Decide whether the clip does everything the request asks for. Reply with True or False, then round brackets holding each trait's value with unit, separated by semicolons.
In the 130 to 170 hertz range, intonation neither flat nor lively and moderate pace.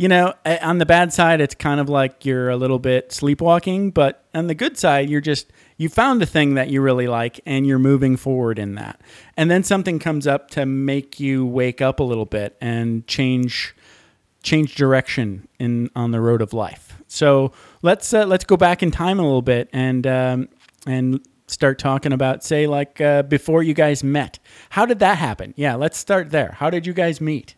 False (140 Hz; 4.1 semitones; 210 wpm)